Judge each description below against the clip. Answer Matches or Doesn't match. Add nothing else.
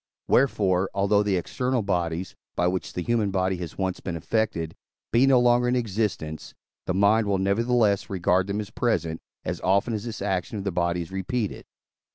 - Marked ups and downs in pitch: Doesn't match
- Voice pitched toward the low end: Matches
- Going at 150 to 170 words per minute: Doesn't match